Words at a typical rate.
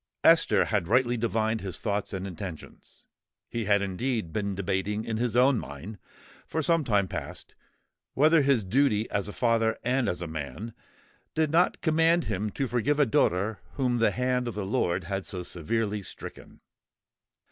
Yes: average, 170 wpm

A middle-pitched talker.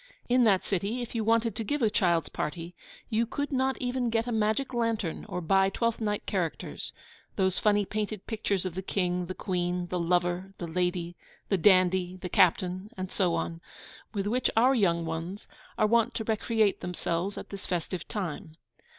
No: high, 195 Hz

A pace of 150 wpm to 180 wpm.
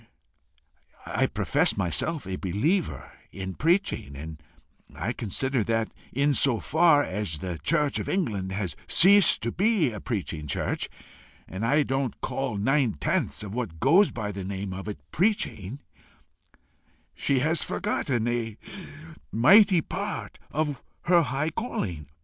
No: slow, 135 wpm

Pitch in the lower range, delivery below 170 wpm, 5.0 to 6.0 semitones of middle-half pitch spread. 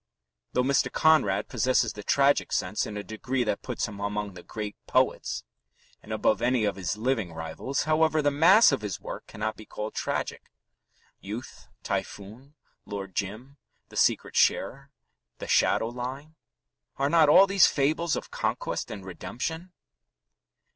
Yes: low, 120 Hz; average, 155 wpm; wide, 5.5 semitones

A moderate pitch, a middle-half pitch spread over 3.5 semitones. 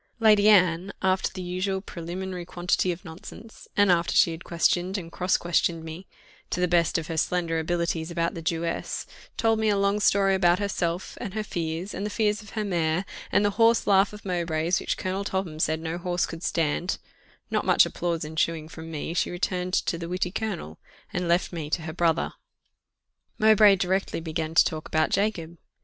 No: medium, 175 Hz; average, 2.9 semitones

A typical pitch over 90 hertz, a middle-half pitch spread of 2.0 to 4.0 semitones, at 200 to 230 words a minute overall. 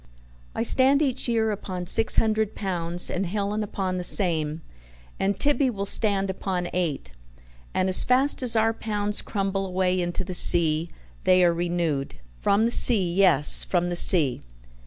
No: high, 190 Hz; average, 3.6 semitones; average, 160 wpm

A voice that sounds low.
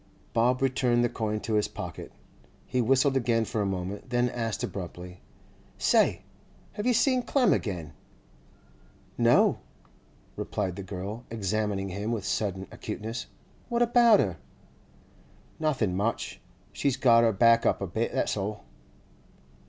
Yes: low, 115 Hz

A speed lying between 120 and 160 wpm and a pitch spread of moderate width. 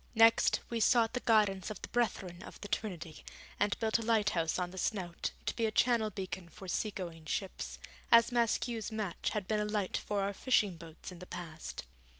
No: average, 200 wpm; average, 3.7 semitones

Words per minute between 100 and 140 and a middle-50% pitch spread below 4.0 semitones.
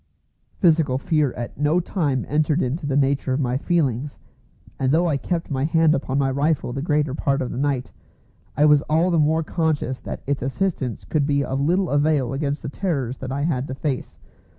No: average, 200 wpm; average, 2.8 semitones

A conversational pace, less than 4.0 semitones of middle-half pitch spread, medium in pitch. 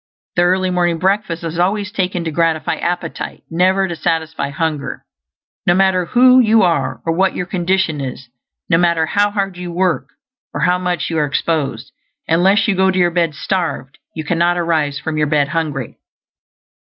Yes: average, 175 wpm; narrow, 2.6 semitones; medium, 175 Hz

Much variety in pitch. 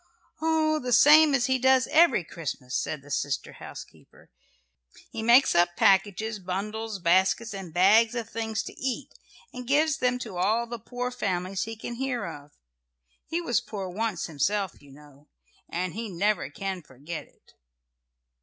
Yes: wide, 5.7 semitones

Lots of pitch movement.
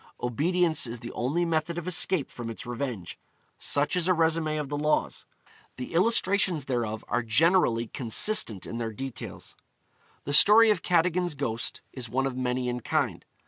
Yes: wide, 6.1 semitones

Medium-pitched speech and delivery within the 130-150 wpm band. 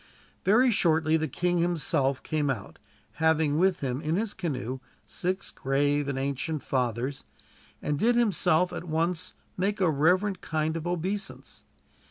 Yes: medium, 160 Hz; average, 145 wpm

